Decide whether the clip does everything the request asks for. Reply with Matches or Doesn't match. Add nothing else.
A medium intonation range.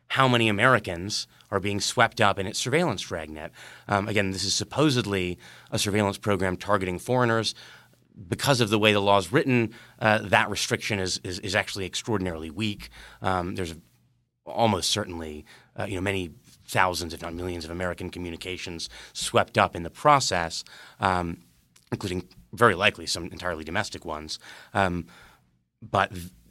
Matches